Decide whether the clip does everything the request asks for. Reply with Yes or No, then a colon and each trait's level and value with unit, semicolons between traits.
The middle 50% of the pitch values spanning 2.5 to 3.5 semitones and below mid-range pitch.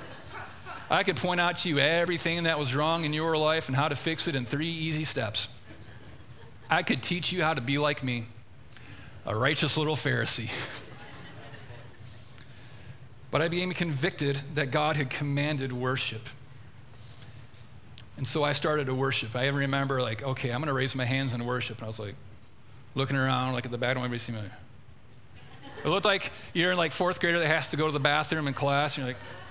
No: average, 4.3 semitones; low, 130 Hz